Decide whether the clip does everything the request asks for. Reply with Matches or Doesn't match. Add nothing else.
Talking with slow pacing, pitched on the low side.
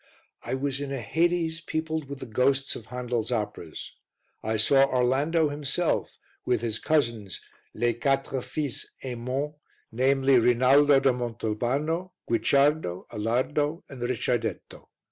Matches